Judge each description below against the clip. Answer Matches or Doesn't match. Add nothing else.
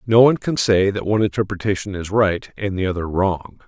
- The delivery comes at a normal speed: Doesn't match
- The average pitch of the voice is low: Matches